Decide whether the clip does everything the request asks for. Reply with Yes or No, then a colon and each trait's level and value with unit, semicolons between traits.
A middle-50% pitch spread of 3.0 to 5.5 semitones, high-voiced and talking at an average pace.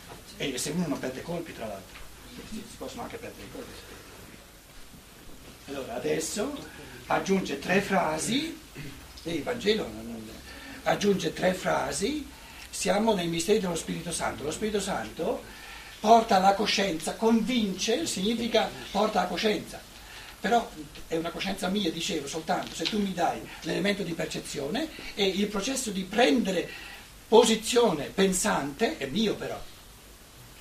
Yes: average, 4.9 semitones; high, 195 Hz; average, 140 wpm